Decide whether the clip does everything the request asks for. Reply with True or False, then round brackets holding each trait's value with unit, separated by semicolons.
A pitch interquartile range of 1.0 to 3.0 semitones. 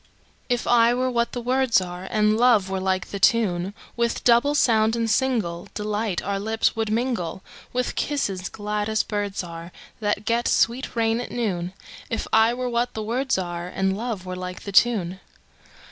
False (3.8 semitones)